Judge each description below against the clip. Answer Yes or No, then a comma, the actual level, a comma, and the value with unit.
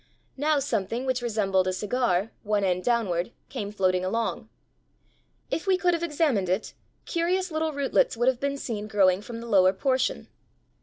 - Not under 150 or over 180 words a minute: Yes, average, 165 wpm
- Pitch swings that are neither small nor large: No, wide, 6.4 semitones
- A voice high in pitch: Yes, high, 230 Hz